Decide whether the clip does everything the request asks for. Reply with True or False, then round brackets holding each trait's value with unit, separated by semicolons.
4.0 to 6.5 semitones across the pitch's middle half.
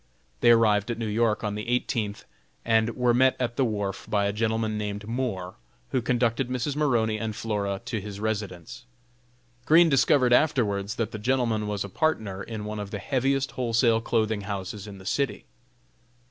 False (2.9 semitones)